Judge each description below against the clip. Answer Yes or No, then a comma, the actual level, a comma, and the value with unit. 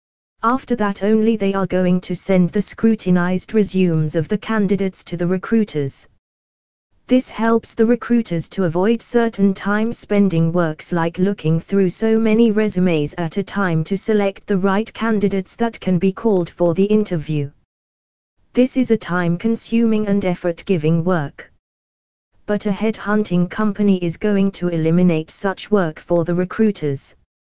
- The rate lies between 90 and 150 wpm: Yes, average, 145 wpm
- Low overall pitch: No, high, 190 Hz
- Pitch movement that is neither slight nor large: Yes, average, 4.0 semitones